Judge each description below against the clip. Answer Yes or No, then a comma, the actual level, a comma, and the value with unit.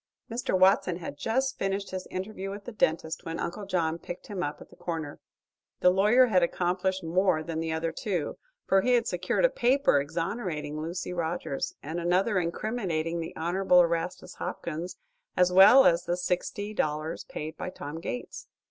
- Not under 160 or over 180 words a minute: Yes, average, 175 wpm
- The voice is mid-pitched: Yes, medium, 180 Hz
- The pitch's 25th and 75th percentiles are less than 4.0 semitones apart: Yes, average, 3.1 semitones